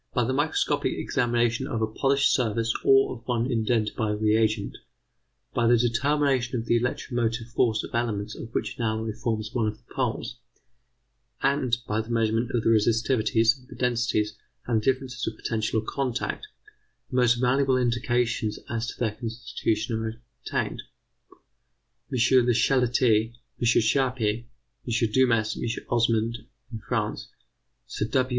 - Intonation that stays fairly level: Yes, narrow, 1.9 semitones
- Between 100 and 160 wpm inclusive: Yes, average, 150 wpm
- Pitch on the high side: No, low, 115 Hz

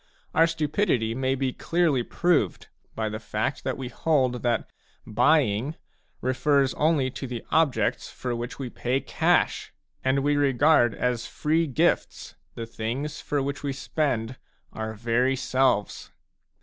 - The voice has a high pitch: No, low, 130 Hz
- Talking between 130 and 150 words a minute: Yes, average, 140 wpm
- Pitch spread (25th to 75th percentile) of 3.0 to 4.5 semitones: Yes, average, 3.5 semitones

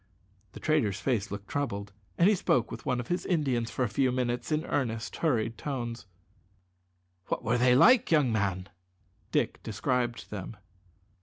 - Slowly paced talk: No, average, 160 wpm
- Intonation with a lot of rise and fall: No, average, 4.4 semitones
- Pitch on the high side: No, low, 120 Hz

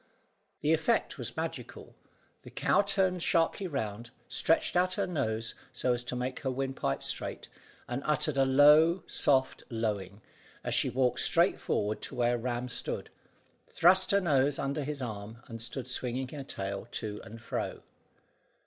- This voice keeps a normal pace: Yes, average, 160 wpm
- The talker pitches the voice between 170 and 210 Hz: No, low, 130 Hz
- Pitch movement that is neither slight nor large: Yes, average, 4.8 semitones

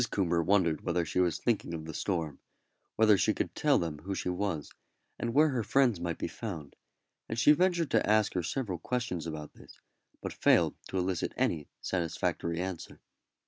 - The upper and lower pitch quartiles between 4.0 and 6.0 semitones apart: Yes, average, 5.0 semitones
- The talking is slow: No, average, 185 wpm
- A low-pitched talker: Yes, very low, 90 Hz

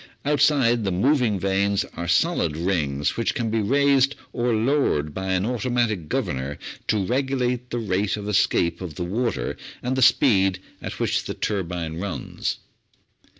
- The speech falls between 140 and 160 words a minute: Yes, average, 150 wpm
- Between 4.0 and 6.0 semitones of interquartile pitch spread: Yes, wide, 5.6 semitones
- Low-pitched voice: Yes, low, 105 Hz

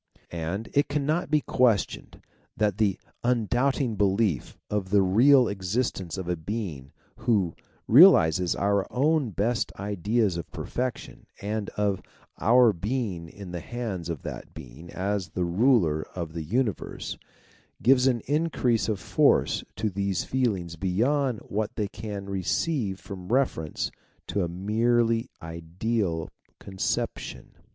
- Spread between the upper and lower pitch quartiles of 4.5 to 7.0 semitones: Yes, average, 5.0 semitones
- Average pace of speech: No, slow, 130 wpm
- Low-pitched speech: Yes, low, 105 Hz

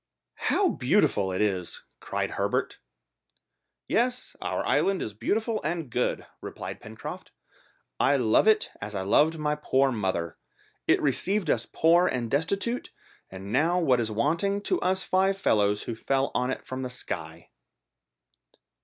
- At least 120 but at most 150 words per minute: Yes, average, 145 wpm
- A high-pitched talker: No, medium, 140 Hz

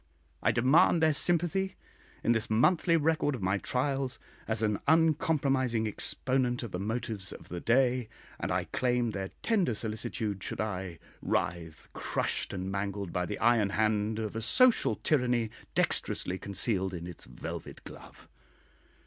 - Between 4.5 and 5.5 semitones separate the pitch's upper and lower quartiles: Yes, average, 5.2 semitones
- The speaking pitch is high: No, low, 115 Hz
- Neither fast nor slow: Yes, average, 150 wpm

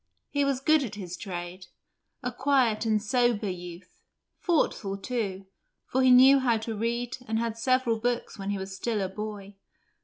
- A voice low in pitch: No, high, 225 Hz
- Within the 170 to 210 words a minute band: Yes, average, 180 wpm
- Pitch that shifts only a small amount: No, average, 4.2 semitones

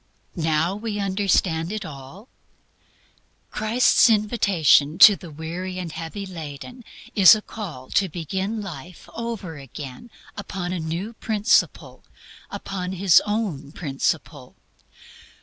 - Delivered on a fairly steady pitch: No, average, 4.5 semitones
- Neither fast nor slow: No, slow, 115 wpm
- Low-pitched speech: No, medium, 185 Hz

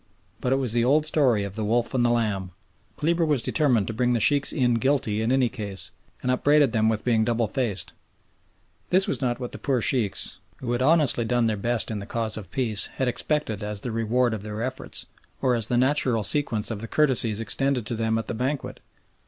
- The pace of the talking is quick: Yes, fast, 220 wpm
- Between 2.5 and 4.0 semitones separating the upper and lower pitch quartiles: Yes, average, 3.1 semitones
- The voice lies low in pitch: Yes, low, 120 Hz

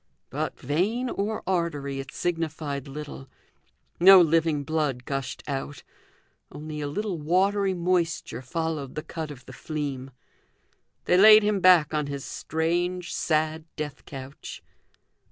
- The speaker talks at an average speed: No, slow, 130 wpm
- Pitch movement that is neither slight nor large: Yes, average, 3.8 semitones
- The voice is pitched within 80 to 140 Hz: No, medium, 155 Hz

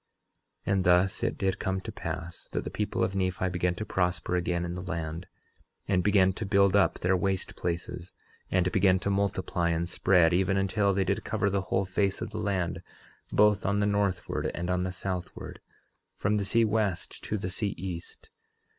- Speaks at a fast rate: No, average, 195 wpm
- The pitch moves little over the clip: Yes, narrow, 1.8 semitones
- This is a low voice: Yes, very low, 95 Hz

